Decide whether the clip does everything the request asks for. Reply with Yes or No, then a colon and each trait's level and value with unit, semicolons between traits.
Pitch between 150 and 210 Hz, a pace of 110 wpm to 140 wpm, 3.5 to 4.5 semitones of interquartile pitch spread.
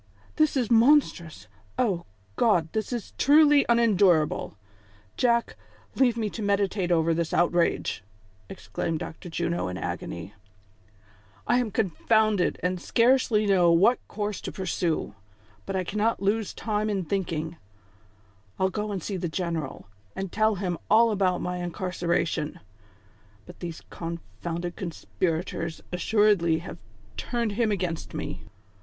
Yes: high, 190 Hz; slow, 135 wpm; average, 4.2 semitones